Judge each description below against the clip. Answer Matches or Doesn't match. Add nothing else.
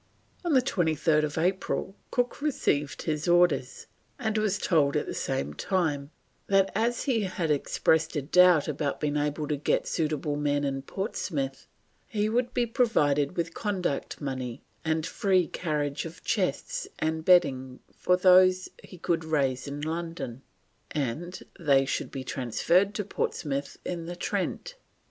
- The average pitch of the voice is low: Doesn't match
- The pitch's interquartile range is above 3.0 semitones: Matches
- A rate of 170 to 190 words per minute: Doesn't match